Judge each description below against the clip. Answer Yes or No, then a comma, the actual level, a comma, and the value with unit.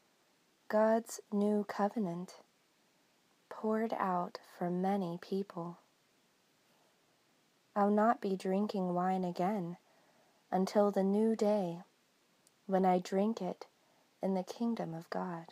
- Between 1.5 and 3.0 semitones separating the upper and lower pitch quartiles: Yes, narrow, 2.6 semitones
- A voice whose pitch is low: No, high, 195 Hz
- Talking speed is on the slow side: Yes, slow, 105 wpm